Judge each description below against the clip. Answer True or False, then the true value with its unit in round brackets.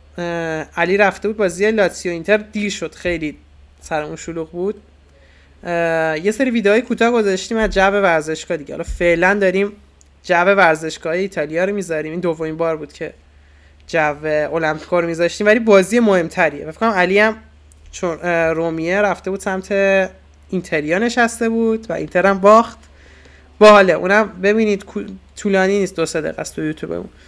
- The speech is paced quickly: False (145 wpm)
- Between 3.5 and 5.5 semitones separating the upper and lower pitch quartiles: True (4.4 semitones)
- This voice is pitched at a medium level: True (175 Hz)